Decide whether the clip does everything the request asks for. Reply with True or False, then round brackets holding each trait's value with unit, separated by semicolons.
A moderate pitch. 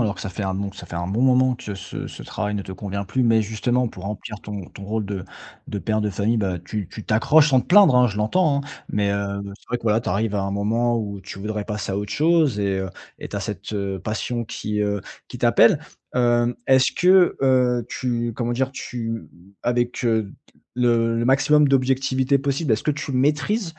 False (115 Hz)